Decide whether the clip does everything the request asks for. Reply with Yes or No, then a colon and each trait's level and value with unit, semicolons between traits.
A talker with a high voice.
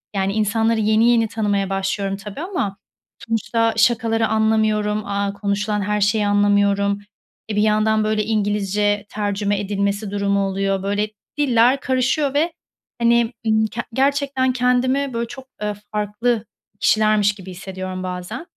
Yes: high, 210 Hz